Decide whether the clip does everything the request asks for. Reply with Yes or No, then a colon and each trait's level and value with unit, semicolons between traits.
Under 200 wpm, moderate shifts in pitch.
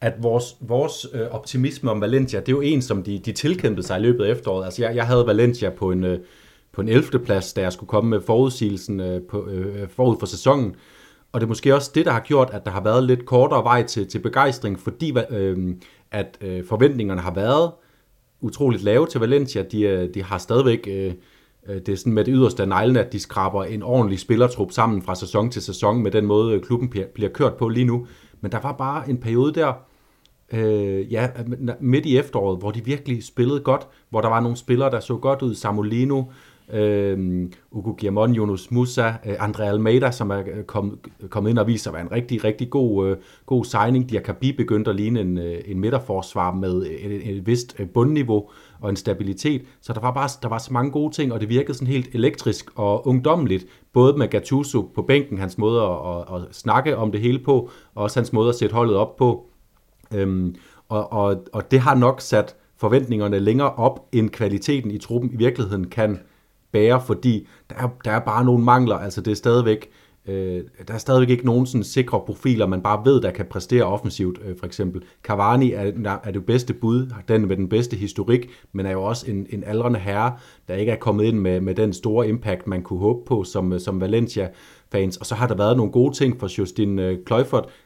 No: average, 210 wpm; average, 3.9 semitones